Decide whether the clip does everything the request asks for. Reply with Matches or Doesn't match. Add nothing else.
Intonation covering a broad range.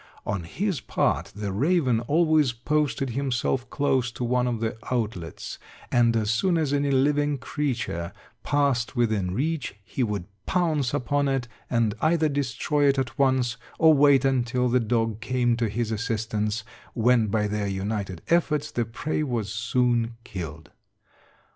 Doesn't match